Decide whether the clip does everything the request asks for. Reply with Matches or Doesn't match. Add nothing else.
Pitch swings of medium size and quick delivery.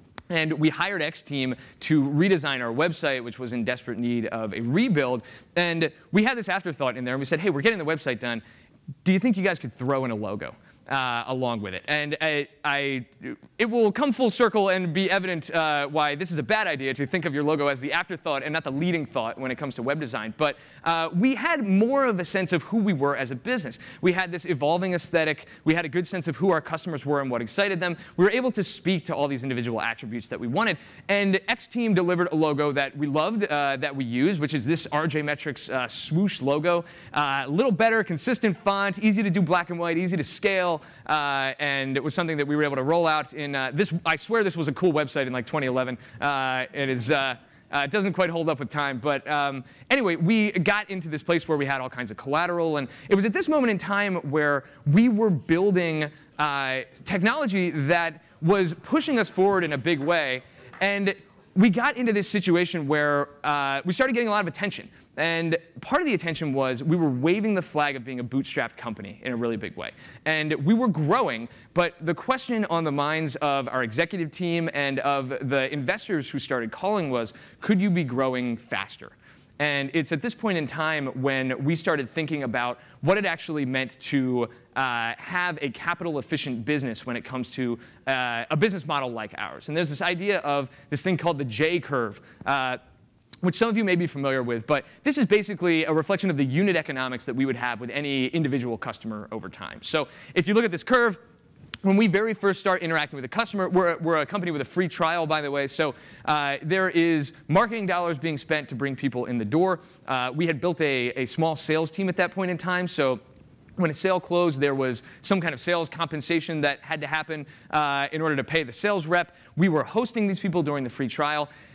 Matches